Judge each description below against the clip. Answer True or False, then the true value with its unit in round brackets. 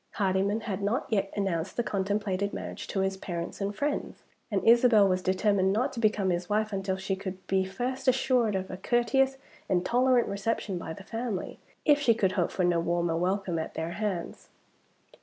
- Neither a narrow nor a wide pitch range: True (3.3 semitones)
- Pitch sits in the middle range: False (200 Hz)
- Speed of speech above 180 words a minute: True (190 wpm)